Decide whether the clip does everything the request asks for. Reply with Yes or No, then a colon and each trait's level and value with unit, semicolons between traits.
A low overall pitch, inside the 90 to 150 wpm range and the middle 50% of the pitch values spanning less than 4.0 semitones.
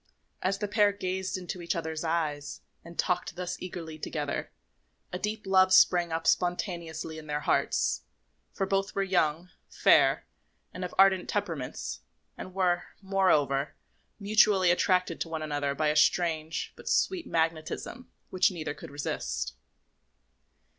No: medium, 175 Hz; average, 140 wpm; average, 3.1 semitones